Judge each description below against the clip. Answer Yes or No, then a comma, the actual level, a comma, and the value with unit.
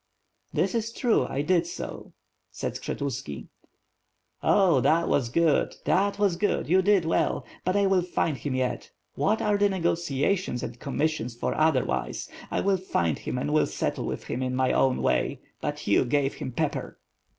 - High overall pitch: No, medium, 155 Hz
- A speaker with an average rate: Yes, average, 175 wpm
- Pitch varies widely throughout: Yes, wide, 6.5 semitones